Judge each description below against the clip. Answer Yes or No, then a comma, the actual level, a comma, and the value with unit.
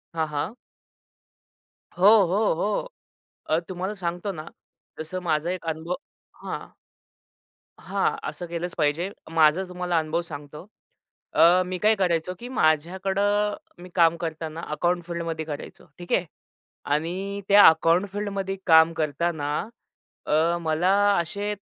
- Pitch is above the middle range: No, medium, 170 Hz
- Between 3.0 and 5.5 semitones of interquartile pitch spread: No, narrow, 2.6 semitones